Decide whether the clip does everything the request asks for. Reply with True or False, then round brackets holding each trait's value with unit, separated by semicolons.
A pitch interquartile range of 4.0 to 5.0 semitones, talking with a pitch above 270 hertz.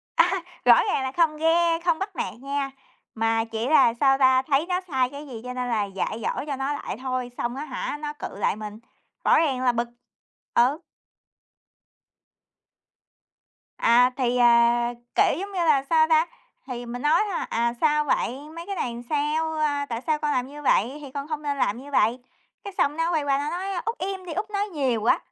True (4.5 semitones; 280 Hz)